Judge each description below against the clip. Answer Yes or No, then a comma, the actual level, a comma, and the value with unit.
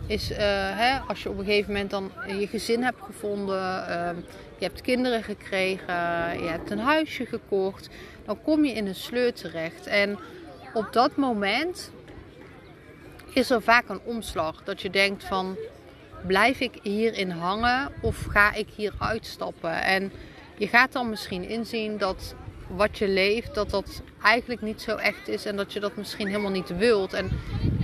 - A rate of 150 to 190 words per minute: Yes, average, 170 wpm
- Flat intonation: No, average, 3.2 semitones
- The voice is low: No, high, 205 Hz